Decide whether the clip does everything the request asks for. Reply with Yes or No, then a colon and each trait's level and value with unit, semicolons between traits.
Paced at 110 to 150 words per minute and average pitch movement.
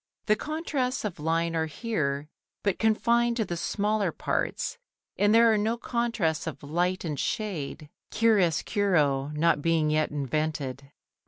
No: average, 140 wpm; wide, 6.4 semitones